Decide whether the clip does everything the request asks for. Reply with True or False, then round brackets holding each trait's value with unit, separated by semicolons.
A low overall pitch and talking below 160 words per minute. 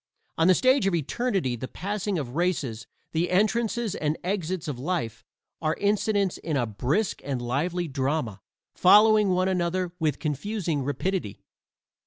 False (175 Hz; 145 wpm)